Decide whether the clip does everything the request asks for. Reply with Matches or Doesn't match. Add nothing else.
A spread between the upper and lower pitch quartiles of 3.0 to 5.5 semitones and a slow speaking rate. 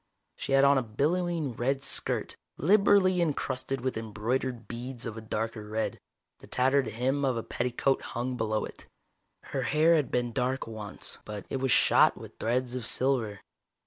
Doesn't match